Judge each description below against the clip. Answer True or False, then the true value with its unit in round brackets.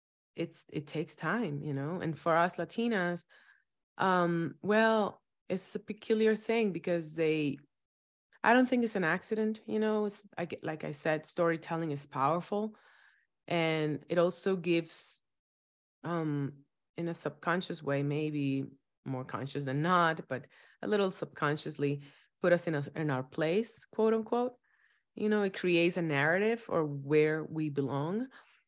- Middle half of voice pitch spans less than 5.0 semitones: False (5.5 semitones)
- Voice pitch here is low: False (165 Hz)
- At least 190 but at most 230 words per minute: False (150 wpm)